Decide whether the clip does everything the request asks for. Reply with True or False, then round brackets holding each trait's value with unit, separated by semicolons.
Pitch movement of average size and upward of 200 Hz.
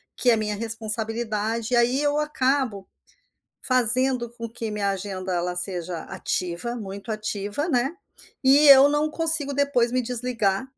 True (4.3 semitones; 235 Hz)